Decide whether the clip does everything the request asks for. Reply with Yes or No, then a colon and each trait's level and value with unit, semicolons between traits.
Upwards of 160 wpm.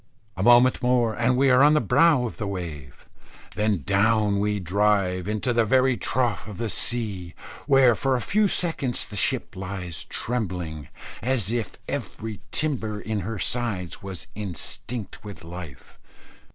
No: average, 155 wpm